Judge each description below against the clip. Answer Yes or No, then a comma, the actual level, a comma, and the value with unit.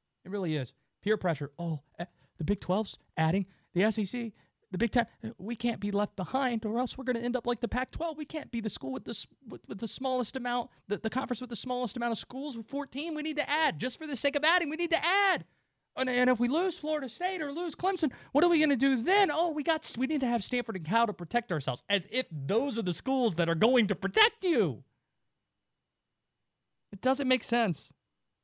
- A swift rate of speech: Yes, fast, 240 wpm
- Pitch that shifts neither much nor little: No, wide, 6.3 semitones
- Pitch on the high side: Yes, high, 240 Hz